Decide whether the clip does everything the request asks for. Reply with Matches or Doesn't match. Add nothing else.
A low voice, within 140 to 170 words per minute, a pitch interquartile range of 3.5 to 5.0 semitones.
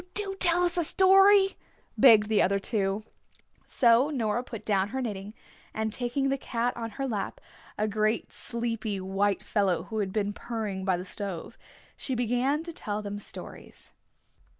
Doesn't match